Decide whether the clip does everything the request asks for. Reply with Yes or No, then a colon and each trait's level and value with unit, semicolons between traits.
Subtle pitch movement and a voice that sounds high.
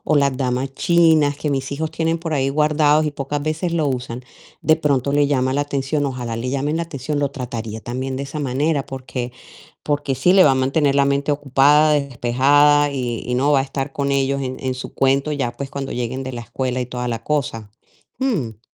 No: narrow, 2.2 semitones; medium, 140 Hz